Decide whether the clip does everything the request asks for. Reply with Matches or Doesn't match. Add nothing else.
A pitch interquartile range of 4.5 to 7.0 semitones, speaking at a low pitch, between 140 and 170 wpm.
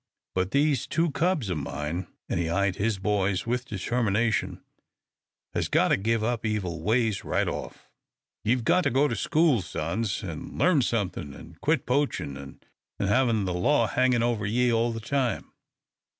Matches